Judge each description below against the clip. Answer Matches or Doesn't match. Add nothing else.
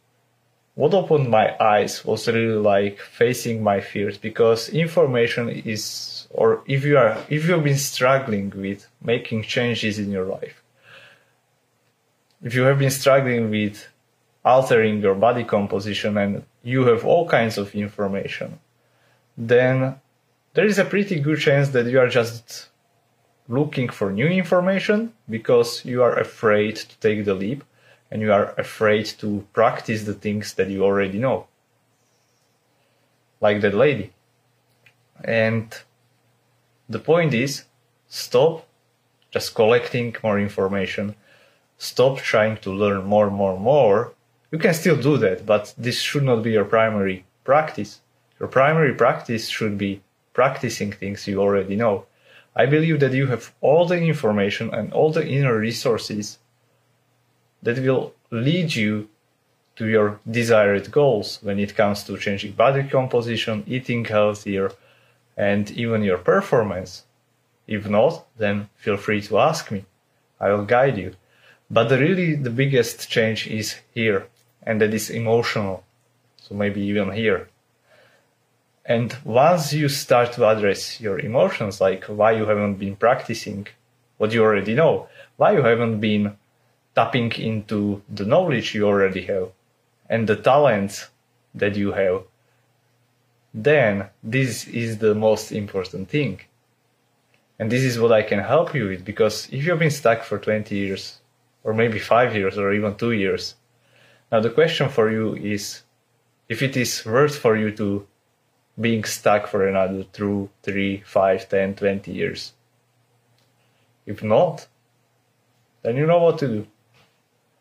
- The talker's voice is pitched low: Matches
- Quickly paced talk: Doesn't match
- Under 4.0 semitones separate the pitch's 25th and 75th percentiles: Matches